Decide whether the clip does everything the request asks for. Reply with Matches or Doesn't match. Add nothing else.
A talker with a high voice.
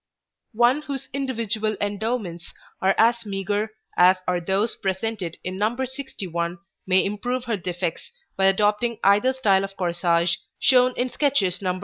Matches